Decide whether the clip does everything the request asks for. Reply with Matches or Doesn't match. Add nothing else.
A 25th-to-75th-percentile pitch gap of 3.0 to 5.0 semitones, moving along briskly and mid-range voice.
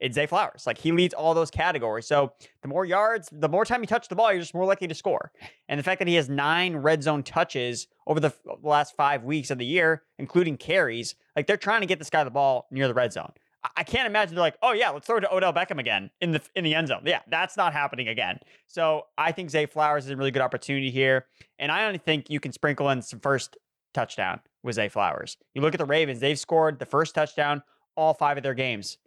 Matches